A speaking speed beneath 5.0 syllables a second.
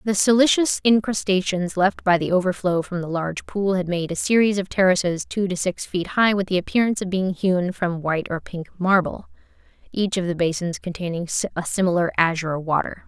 No: 5.4 syllables/s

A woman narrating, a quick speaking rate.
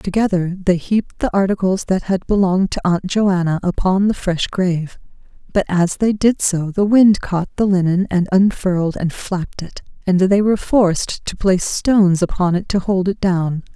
No: female; average, 190 wpm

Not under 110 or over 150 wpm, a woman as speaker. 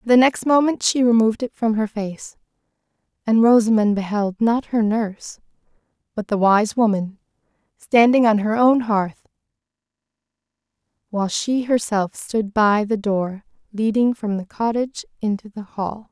Yes: slow, 135 wpm; female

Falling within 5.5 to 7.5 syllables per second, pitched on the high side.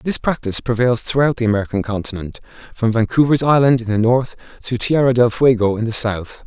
No: 5.8 syllables/s; low, 120 Hz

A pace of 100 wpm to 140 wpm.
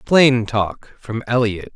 Yes: slow, 135 wpm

